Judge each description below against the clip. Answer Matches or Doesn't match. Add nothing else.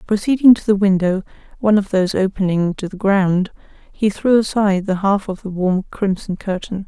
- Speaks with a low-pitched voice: Doesn't match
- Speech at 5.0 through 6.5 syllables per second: Matches